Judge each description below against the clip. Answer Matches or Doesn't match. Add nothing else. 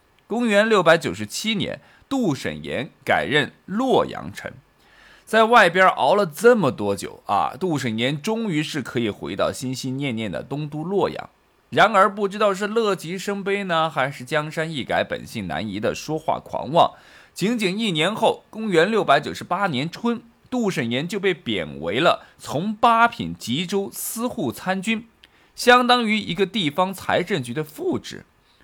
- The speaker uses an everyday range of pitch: Doesn't match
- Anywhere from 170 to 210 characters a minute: Doesn't match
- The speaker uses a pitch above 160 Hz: Matches